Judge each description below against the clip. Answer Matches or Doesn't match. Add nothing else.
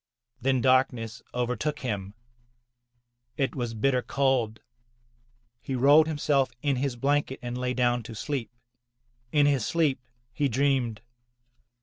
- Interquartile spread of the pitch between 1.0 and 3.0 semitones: Matches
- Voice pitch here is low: Matches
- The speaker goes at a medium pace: Doesn't match